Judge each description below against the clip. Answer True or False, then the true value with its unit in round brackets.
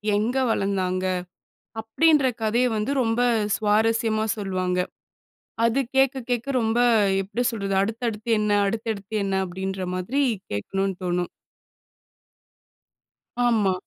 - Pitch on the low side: False (215 Hz)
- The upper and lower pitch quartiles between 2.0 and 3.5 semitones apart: True (3.2 semitones)